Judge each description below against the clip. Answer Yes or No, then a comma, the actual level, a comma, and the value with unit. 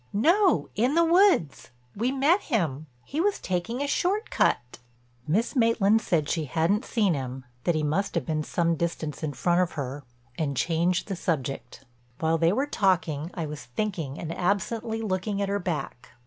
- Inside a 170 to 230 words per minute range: Yes, average, 175 wpm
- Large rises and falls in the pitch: Yes, wide, 6.4 semitones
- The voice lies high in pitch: No, medium, 175 Hz